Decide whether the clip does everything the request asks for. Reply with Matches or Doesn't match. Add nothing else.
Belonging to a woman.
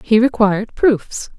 Matches